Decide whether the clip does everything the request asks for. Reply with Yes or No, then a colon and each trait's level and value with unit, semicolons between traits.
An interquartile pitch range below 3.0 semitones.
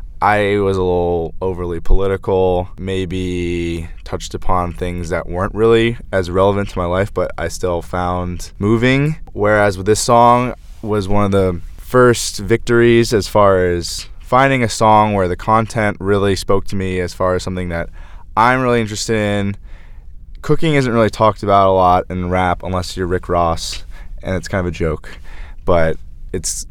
No: average, 3.4 semitones